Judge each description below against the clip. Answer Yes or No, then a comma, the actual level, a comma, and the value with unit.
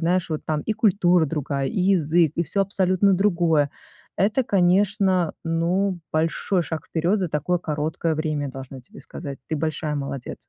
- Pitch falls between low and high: Yes, medium, 170 Hz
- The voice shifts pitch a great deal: No, average, 3.7 semitones